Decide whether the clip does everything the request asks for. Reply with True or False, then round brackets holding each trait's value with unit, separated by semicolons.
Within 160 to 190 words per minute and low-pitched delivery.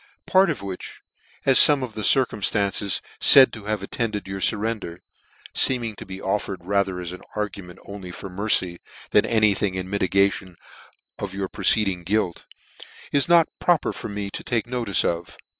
True (165 wpm; 100 Hz)